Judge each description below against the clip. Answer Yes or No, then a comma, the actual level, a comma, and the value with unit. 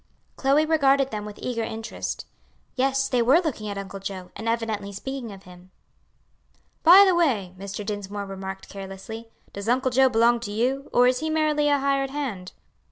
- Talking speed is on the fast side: No, average, 175 wpm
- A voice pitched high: Yes, high, 230 Hz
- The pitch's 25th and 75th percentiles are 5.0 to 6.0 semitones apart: Yes, average, 5.3 semitones